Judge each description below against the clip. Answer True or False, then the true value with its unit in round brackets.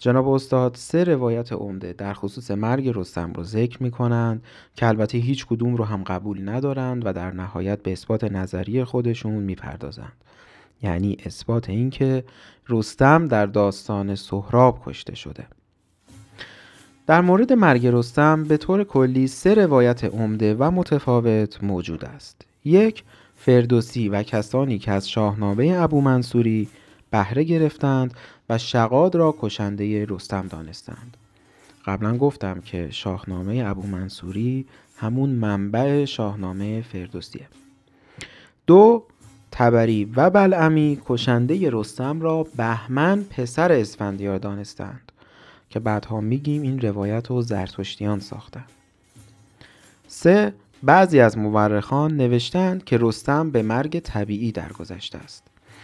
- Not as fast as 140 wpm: True (120 wpm)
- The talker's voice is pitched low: True (115 Hz)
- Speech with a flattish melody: False (4.8 semitones)